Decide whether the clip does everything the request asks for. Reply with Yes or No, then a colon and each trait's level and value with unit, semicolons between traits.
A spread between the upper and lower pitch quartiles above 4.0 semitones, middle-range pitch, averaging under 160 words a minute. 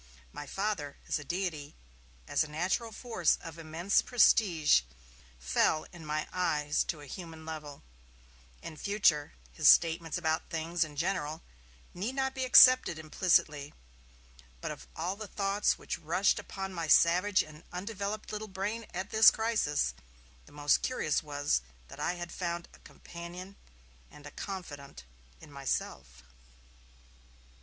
Yes: average, 4.7 semitones; medium, 170 Hz; average, 140 wpm